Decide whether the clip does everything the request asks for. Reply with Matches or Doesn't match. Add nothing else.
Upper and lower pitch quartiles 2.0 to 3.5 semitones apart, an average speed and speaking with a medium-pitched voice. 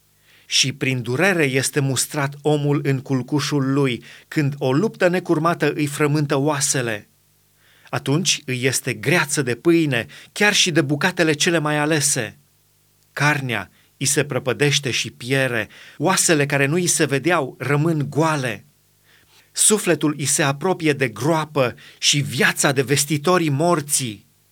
Matches